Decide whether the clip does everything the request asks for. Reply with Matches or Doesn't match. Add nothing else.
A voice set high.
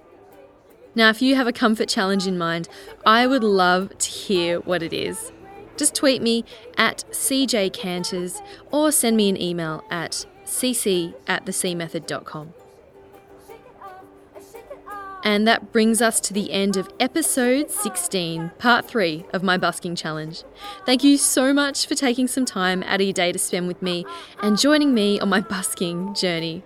Matches